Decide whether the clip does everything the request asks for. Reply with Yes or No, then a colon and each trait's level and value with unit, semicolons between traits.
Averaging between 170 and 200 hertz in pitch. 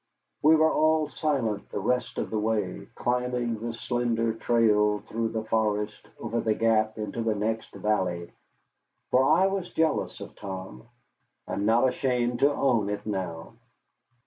No: low, 115 Hz